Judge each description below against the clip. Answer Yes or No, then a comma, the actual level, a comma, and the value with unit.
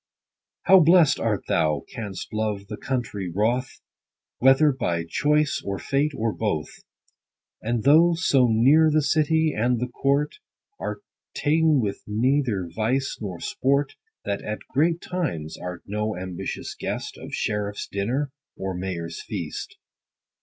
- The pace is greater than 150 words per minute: No, average, 140 wpm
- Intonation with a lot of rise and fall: Yes, wide, 6.5 semitones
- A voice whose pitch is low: Yes, low, 120 Hz